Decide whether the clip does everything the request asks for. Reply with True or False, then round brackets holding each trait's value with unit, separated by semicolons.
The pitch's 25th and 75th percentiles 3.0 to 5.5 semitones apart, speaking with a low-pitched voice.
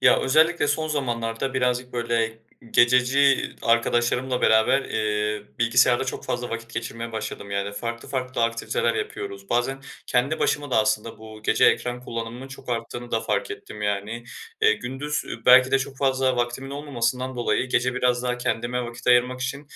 False (2.4 semitones; 125 Hz)